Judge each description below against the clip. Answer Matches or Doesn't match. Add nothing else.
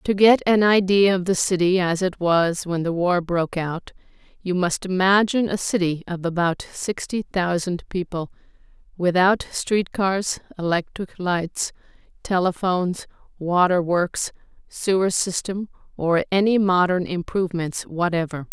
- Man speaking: Doesn't match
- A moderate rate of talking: Doesn't match